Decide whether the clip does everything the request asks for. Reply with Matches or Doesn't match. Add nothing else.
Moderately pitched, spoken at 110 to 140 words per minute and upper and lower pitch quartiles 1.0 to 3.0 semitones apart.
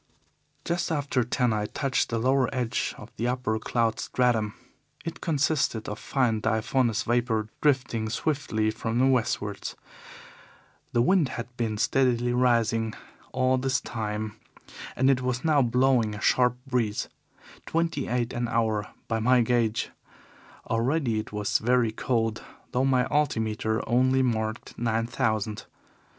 Doesn't match